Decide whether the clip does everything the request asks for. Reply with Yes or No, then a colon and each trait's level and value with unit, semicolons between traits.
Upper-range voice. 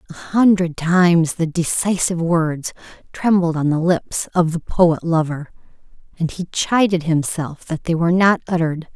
No: medium, 170 Hz